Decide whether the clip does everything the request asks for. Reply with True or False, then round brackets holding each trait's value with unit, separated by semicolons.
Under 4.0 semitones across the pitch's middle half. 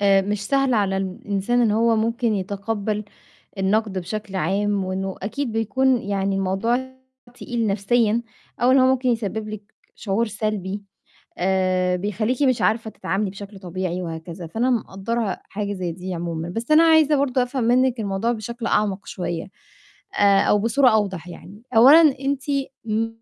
True (3.5 semitones)